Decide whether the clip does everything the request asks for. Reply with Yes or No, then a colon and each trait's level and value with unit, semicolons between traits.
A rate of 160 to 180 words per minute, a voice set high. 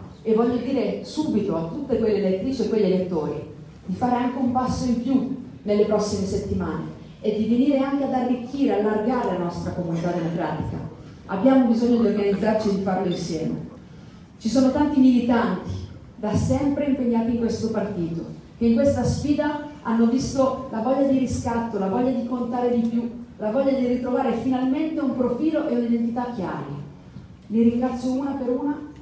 Yes: fast, 170 wpm; high, 240 Hz